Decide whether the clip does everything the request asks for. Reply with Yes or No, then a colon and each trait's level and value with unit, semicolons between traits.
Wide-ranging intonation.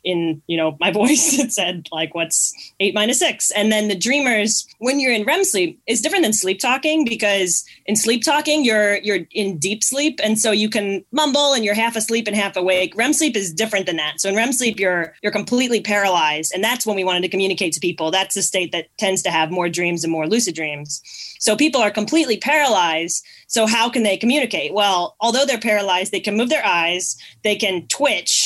No: average, 4.4 semitones